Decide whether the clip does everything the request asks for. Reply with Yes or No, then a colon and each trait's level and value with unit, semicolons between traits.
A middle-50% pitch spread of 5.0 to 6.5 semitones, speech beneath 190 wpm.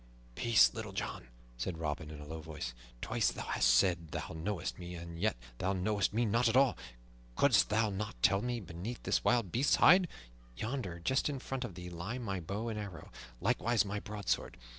No: wide, 5.6 semitones; average, 195 wpm